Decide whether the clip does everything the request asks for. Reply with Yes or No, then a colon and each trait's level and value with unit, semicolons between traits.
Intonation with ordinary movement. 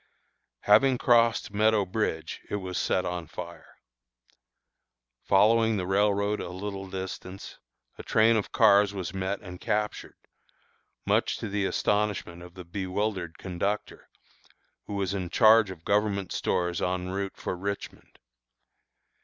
No: narrow, 2.2 semitones